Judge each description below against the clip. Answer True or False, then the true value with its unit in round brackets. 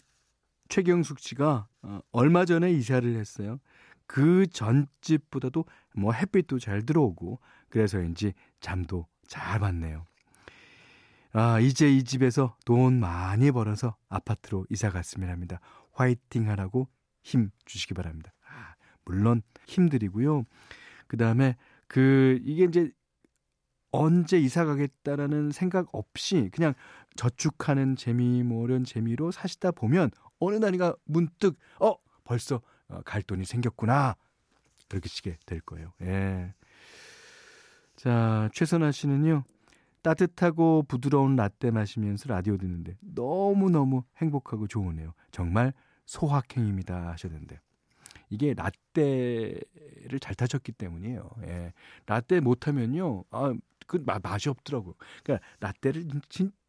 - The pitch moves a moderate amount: False (6.1 semitones)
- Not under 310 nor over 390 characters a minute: False (260 characters per minute)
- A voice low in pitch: True (125 Hz)